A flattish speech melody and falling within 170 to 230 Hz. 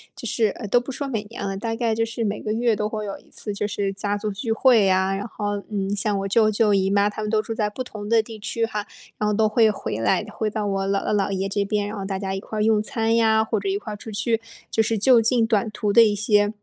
Yes: narrow, 1.8 semitones; high, 210 Hz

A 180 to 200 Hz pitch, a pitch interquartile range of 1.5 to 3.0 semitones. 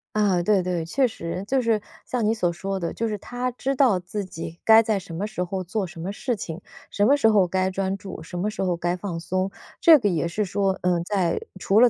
No: high, 195 Hz; average, 3.5 semitones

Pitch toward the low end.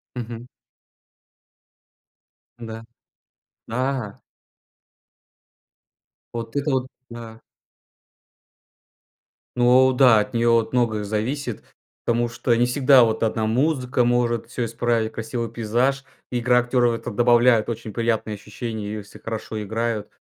Yes: low, 115 Hz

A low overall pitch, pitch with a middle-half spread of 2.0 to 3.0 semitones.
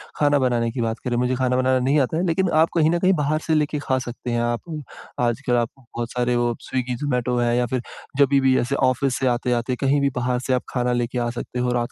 Yes: low, 125 Hz; narrow, 2.4 semitones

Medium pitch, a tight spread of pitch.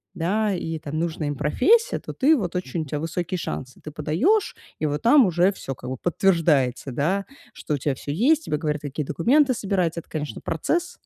No: medium, 165 Hz; wide, 5.6 semitones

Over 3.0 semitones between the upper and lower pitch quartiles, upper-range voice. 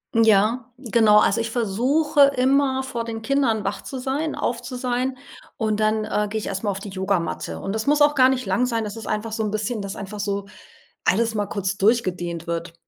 Yes: average, 3.9 semitones; high, 220 Hz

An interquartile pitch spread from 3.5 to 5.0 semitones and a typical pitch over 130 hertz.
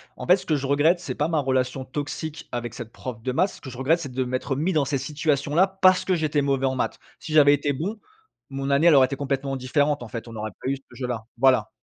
No: average, 3.1 semitones; medium, 140 Hz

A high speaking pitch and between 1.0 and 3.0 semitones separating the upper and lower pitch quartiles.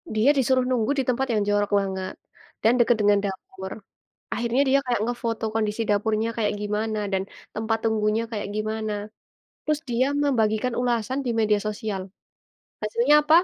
Yes: high, 220 Hz; narrow, 2.4 semitones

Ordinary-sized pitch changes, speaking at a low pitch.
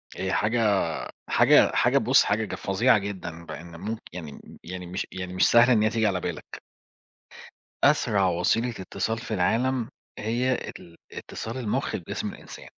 Yes: average, 4.0 semitones; low, 100 Hz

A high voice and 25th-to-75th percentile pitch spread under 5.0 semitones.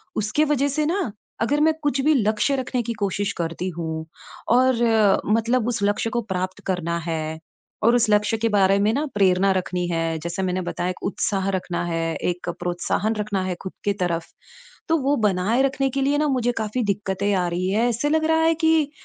No: high, 210 Hz; wide, 5.6 semitones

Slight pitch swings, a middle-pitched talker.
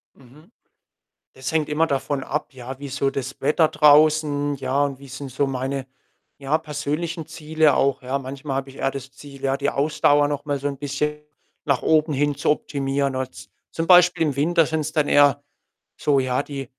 Yes: narrow, 1.9 semitones; medium, 145 Hz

